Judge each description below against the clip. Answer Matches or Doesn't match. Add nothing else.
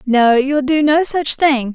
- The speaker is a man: Doesn't match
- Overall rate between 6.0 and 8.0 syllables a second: Doesn't match